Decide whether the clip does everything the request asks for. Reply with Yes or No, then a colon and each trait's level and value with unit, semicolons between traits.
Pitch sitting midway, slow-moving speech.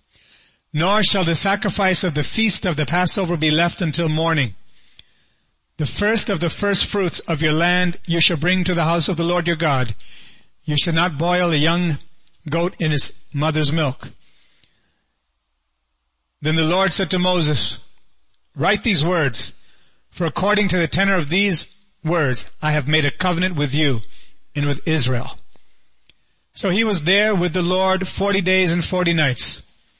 No: medium, 170 Hz; average, 170 wpm